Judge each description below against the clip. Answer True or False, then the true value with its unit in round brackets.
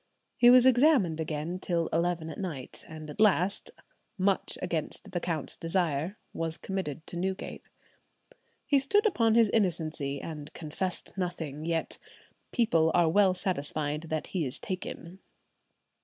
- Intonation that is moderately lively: True (3.5 semitones)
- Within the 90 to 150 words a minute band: True (140 wpm)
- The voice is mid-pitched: True (175 Hz)